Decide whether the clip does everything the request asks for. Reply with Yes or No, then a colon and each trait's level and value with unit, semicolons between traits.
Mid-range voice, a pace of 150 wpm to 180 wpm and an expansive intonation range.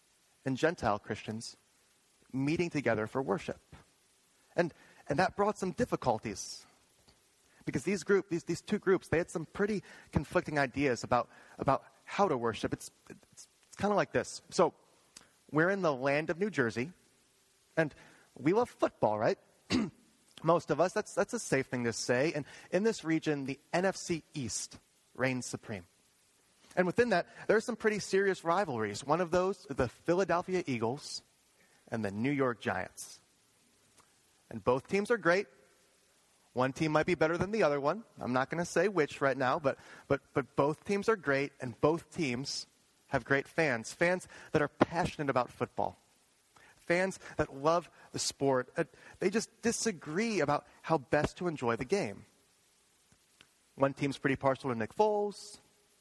Yes: medium, 150 Hz; average, 165 wpm; wide, 5.8 semitones